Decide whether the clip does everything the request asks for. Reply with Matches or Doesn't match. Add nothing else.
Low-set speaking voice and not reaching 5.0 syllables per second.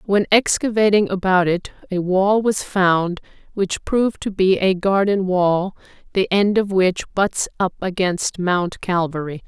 Doesn't match